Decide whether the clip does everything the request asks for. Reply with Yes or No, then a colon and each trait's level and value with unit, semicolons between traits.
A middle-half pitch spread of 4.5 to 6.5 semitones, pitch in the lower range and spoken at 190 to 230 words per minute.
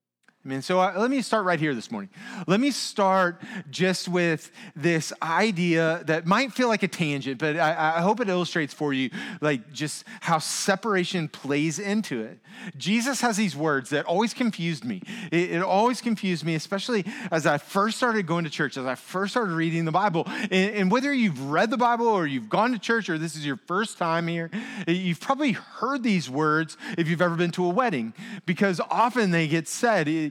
No: average, 5.1 semitones; medium, 185 Hz; fast, 205 wpm